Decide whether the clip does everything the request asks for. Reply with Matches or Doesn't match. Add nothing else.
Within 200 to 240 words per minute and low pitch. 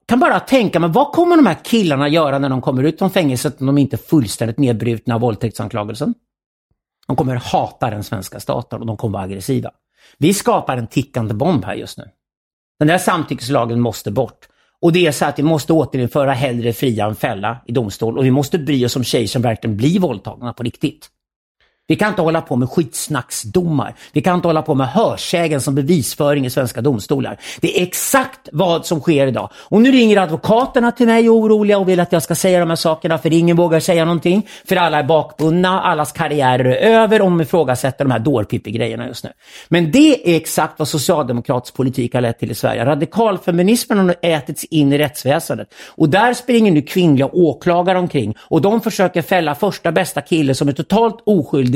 Doesn't match